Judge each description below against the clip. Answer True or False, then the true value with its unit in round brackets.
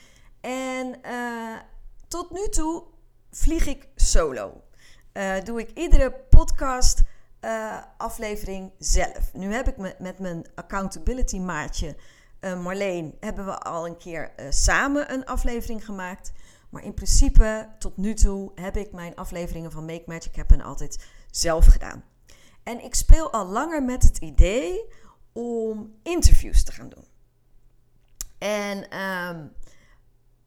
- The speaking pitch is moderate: False (210 Hz)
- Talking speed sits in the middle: False (130 wpm)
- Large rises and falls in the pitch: True (5.7 semitones)